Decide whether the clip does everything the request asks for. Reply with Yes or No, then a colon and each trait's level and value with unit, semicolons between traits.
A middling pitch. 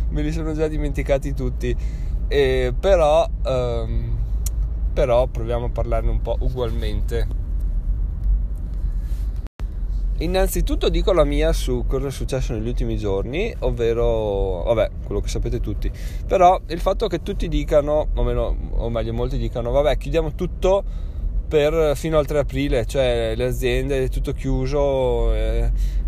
No: low, 120 Hz